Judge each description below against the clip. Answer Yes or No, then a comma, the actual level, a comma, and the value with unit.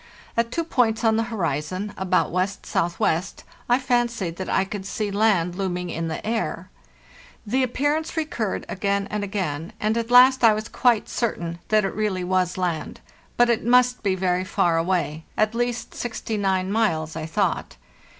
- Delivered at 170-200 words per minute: No, average, 160 wpm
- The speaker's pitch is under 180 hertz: No, high, 205 Hz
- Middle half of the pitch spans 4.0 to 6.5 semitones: Yes, average, 4.4 semitones